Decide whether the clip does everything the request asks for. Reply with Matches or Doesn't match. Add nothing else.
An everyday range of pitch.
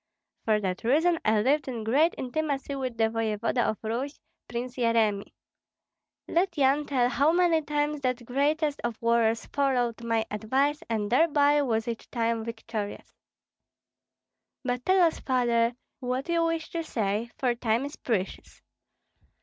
Matches